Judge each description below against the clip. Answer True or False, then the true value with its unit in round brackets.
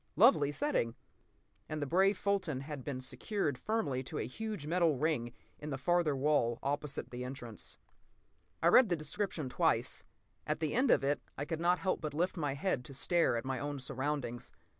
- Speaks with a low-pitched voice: False (150 Hz)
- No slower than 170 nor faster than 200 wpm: True (190 wpm)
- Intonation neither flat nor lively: True (4.9 semitones)